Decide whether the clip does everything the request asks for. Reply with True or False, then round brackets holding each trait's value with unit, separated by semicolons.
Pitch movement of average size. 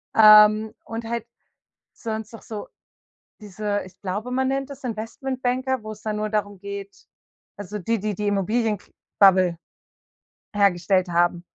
False (2.2 semitones)